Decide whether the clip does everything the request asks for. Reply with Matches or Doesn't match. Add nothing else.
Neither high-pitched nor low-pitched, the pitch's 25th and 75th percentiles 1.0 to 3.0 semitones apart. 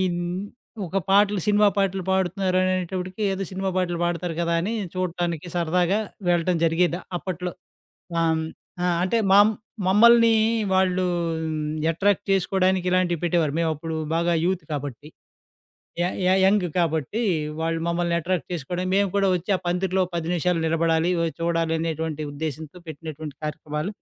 Matches